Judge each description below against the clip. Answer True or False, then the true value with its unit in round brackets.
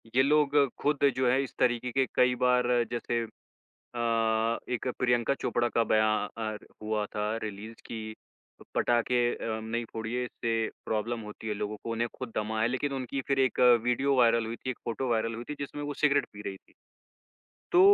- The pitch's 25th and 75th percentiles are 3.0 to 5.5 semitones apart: False (2.5 semitones)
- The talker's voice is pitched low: True (120 Hz)